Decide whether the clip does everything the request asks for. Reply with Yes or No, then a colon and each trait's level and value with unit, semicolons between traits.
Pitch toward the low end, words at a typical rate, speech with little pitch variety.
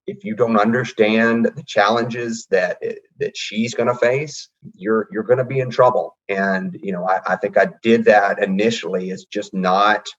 No: low, 115 Hz; average, 195 wpm; average, 3.5 semitones